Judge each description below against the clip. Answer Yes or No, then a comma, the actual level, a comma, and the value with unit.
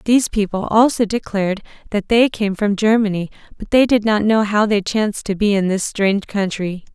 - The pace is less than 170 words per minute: No, average, 200 wpm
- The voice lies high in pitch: Yes, high, 205 Hz